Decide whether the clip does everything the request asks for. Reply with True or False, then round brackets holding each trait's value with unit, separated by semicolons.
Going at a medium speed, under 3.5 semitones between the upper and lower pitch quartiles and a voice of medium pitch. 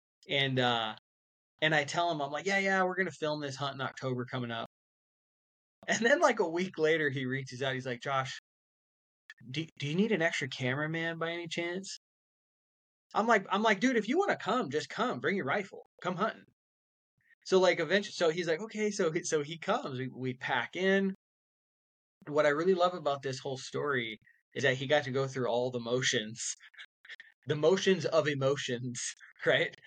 False (195 wpm; 5.5 semitones; 150 Hz)